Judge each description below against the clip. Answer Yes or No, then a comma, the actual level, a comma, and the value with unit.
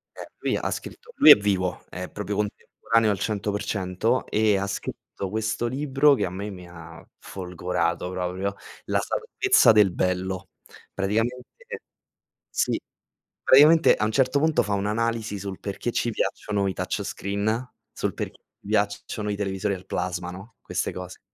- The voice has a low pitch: Yes, low, 100 Hz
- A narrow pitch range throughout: No, average, 3.5 semitones